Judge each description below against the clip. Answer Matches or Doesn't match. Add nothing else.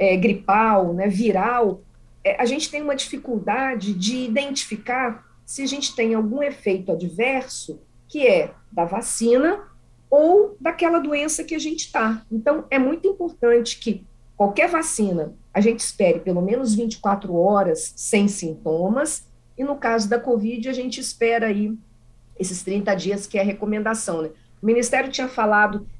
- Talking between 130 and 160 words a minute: Matches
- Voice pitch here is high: Matches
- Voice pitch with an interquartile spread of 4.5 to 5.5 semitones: Matches